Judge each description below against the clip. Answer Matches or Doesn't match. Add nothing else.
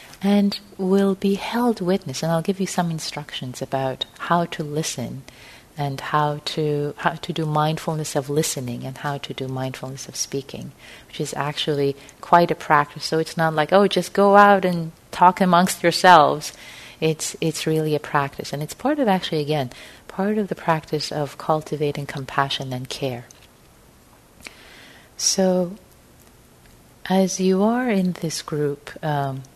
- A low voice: Doesn't match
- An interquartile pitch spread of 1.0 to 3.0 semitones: Doesn't match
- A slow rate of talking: Doesn't match